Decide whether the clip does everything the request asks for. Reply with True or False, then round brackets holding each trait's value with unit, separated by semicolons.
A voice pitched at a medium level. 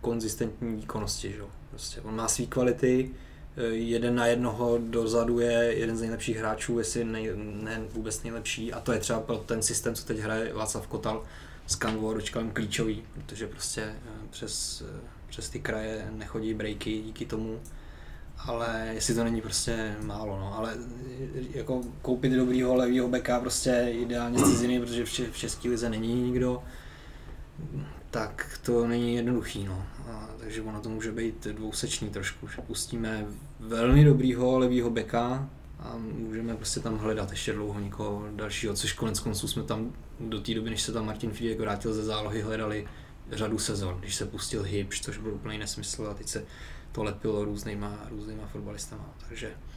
False (110 Hz)